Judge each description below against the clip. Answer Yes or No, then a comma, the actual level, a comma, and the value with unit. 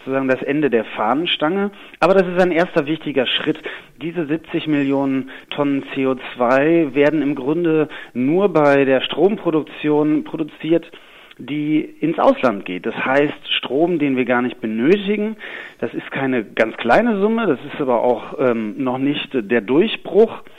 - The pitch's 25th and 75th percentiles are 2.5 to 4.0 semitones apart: No, average, 4.6 semitones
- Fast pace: No, average, 155 wpm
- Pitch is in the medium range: Yes, medium, 150 Hz